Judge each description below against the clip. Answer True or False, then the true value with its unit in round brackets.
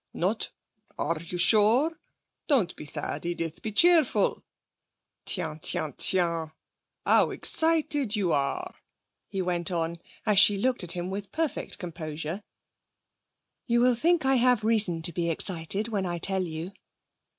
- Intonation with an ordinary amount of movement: False (5.7 semitones)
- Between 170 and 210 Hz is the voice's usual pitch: True (190 Hz)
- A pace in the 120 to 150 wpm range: True (140 wpm)